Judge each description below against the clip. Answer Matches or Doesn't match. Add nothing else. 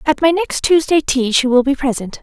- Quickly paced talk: Matches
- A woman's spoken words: Matches